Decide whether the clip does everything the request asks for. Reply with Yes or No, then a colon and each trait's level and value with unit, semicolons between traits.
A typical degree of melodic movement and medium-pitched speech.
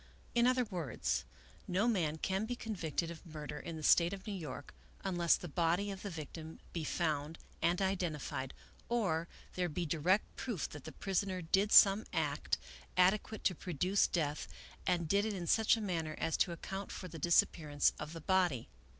Yes: average, 3.6 semitones; medium, 175 Hz